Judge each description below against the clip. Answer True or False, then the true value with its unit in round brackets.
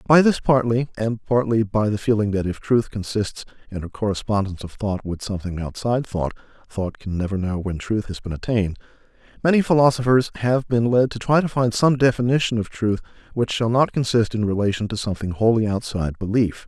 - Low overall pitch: True (110 Hz)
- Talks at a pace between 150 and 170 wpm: False (185 wpm)